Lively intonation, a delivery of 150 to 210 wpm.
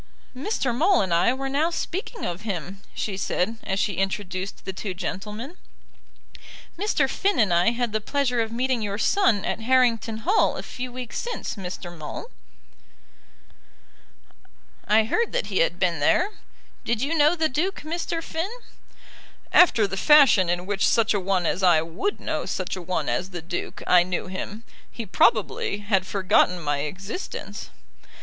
Yes: wide, 6.3 semitones; average, 165 wpm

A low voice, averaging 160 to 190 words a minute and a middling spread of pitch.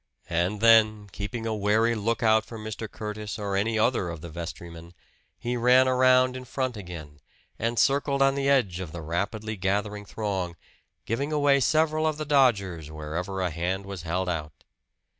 No: low, 105 Hz; average, 170 wpm; wide, 5.7 semitones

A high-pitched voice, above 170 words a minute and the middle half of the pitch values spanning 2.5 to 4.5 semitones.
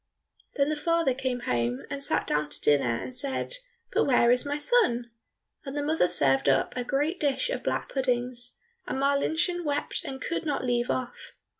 Yes: very high, 265 Hz; average, 185 wpm; average, 3.5 semitones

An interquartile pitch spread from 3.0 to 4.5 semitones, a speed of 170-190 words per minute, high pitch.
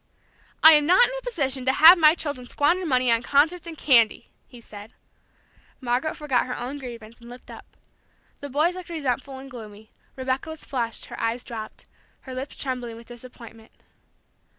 Yes: average, 4.1 semitones; average, 175 wpm; very high, 260 Hz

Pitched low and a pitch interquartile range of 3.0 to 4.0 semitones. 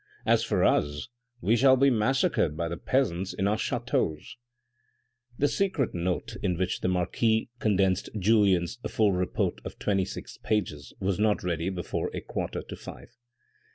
No: low, 100 Hz; average, 4.4 semitones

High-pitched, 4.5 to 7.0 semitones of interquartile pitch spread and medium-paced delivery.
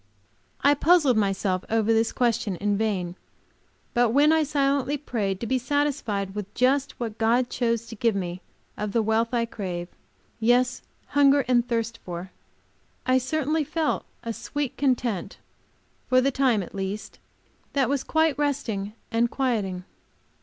Yes: high, 235 Hz; average, 4.8 semitones; average, 150 wpm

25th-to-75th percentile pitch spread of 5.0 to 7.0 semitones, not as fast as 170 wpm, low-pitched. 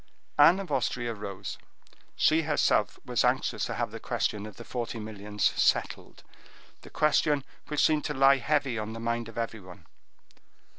Yes: wide, 5.4 semitones; average, 155 wpm; low, 120 Hz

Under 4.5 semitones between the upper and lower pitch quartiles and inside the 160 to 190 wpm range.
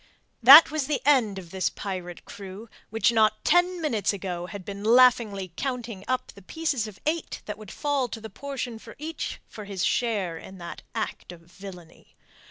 No: average, 5.1 semitones; average, 180 wpm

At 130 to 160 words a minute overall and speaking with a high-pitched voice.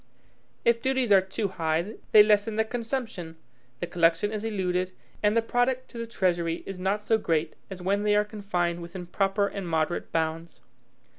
No: average, 175 wpm; high, 195 Hz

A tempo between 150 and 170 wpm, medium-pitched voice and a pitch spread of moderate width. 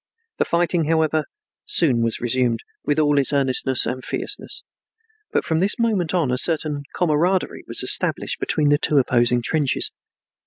Yes: average, 155 wpm; medium, 150 Hz; average, 4.3 semitones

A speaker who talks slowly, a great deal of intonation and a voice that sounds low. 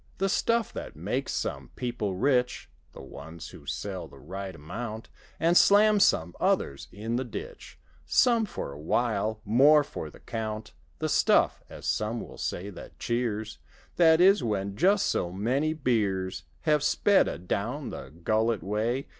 No: average, 155 wpm; wide, 7.3 semitones; low, 115 Hz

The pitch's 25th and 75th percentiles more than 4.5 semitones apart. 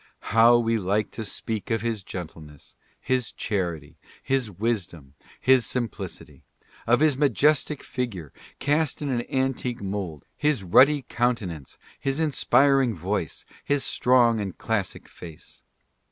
Yes: wide, 5.5 semitones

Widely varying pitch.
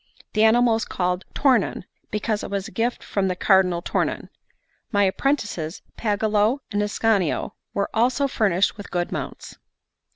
No: average, 2.9 semitones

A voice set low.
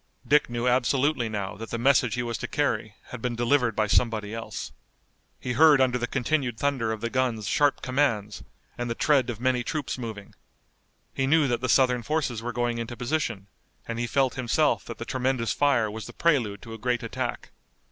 Yes: low, 120 Hz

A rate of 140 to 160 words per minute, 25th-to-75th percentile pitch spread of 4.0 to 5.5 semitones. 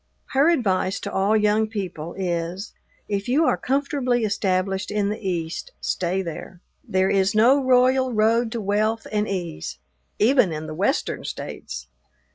Yes: average, 150 wpm; average, 4.3 semitones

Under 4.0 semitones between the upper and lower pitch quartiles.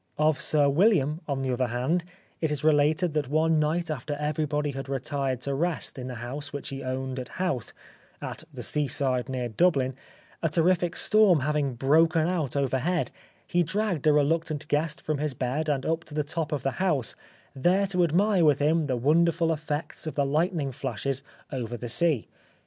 Yes: average, 3.4 semitones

